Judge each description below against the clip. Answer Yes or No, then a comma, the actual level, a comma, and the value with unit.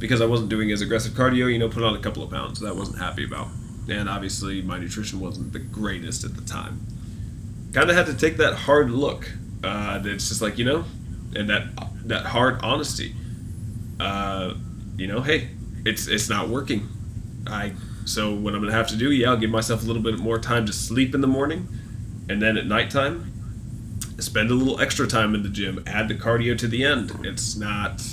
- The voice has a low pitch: Yes, low, 110 Hz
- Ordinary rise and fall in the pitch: No, narrow, 2.1 semitones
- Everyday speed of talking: No, fast, 210 wpm